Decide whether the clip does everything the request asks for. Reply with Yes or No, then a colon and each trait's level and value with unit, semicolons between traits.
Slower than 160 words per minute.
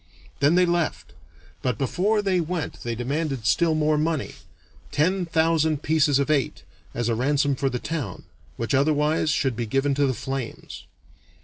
No: average, 165 wpm